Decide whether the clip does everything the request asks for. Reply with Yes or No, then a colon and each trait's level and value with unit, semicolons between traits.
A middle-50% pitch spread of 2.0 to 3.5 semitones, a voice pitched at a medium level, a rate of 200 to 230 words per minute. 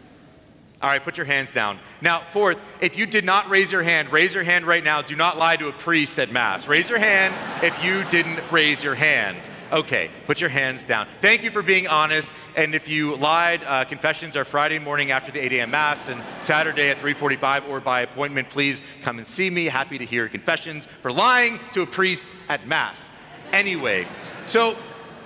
No: average, 4.0 semitones; medium, 155 Hz; fast, 205 wpm